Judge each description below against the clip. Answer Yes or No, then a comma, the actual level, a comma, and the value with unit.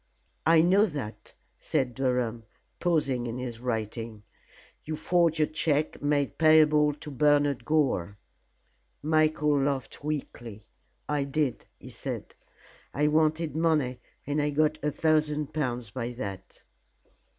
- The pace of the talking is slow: Yes, slow, 125 wpm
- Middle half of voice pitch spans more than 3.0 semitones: Yes, average, 3.8 semitones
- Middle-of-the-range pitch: Yes, medium, 145 Hz